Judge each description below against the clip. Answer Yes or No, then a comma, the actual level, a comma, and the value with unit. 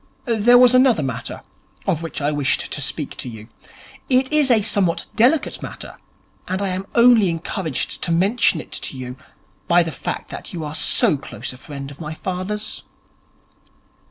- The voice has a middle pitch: Yes, medium, 180 Hz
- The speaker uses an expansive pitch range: Yes, wide, 7.4 semitones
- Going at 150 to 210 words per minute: Yes, average, 175 wpm